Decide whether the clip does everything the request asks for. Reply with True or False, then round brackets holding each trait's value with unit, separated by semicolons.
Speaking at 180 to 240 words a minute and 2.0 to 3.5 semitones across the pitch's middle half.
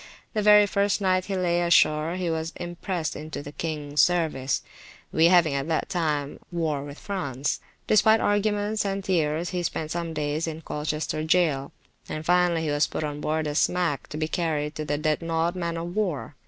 True (185 wpm; 3.0 semitones)